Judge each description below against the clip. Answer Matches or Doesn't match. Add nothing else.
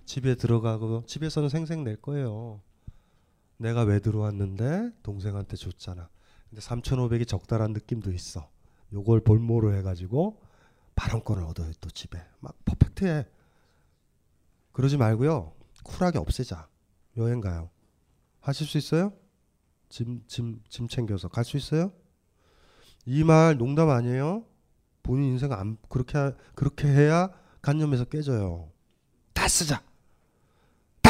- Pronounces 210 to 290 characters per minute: Matches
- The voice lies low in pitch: Matches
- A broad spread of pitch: Matches